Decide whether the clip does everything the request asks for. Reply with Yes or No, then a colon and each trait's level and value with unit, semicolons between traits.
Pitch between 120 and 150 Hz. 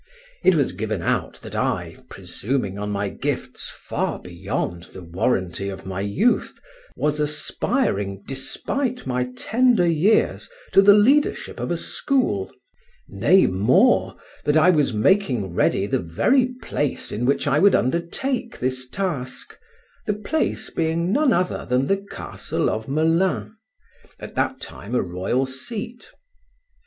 Yes: medium, 140 Hz